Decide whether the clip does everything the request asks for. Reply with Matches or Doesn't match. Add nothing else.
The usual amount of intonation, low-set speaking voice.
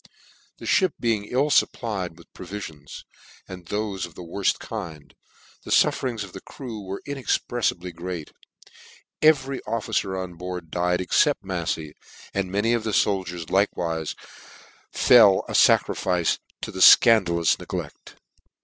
Matches